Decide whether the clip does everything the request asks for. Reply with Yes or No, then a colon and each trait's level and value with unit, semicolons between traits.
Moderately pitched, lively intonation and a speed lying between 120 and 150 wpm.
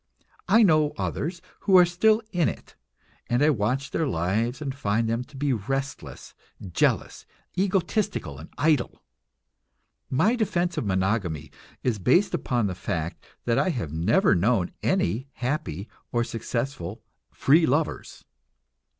No: low, 130 Hz; wide, 7.9 semitones; slow, 135 wpm